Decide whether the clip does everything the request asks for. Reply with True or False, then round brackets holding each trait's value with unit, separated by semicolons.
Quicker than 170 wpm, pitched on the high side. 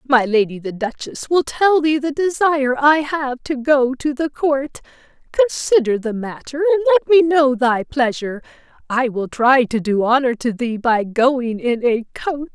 True (180 wpm; 265 Hz)